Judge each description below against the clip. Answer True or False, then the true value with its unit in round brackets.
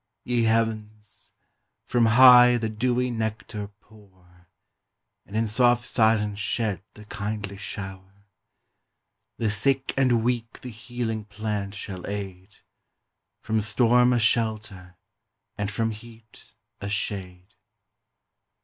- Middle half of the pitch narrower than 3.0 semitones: True (2.6 semitones)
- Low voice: True (110 Hz)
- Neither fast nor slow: False (110 wpm)